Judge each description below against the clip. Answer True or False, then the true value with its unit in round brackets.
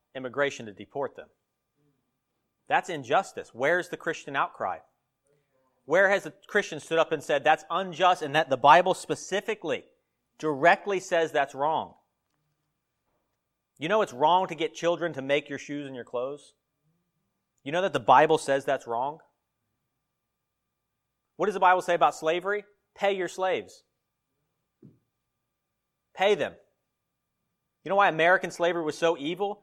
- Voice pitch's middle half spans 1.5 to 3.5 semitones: False (4.1 semitones)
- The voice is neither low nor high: True (160 Hz)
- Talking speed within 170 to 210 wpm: False (145 wpm)